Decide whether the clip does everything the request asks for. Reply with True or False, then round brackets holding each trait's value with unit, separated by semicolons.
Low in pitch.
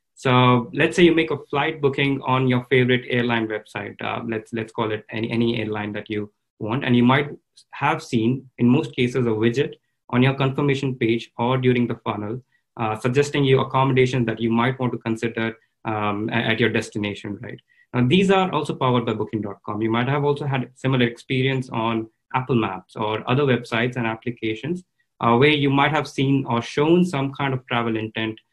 True (125 Hz)